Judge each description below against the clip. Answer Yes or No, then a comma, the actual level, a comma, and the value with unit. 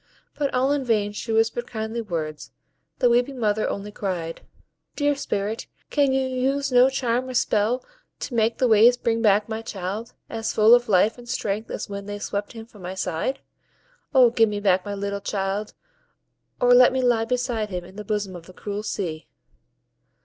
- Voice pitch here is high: Yes, high, 220 Hz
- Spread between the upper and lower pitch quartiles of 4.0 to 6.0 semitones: No, average, 3.4 semitones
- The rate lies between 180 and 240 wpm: Yes, average, 190 wpm